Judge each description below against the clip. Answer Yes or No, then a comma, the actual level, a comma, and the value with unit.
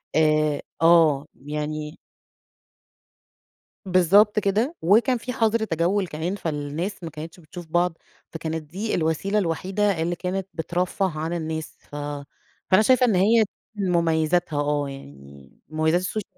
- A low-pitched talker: No, medium, 170 Hz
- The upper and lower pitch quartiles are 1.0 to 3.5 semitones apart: No, average, 3.9 semitones